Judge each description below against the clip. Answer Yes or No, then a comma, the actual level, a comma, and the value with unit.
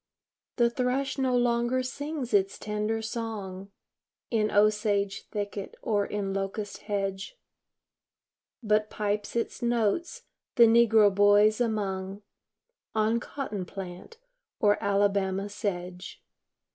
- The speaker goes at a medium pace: No, slow, 105 wpm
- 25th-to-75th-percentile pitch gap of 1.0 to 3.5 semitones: Yes, average, 2.8 semitones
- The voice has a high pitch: Yes, high, 210 Hz